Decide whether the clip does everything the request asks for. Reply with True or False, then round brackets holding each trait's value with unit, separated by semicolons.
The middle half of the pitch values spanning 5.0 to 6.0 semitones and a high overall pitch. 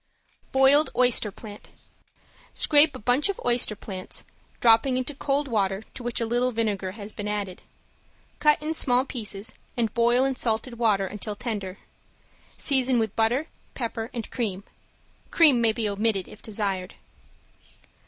False (3.5 semitones; 230 Hz)